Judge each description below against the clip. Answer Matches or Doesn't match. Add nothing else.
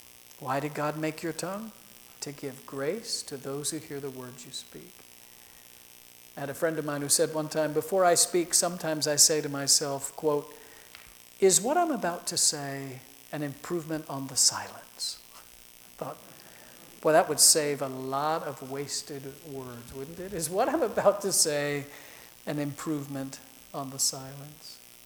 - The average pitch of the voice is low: Doesn't match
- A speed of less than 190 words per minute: Matches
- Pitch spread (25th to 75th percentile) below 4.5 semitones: Matches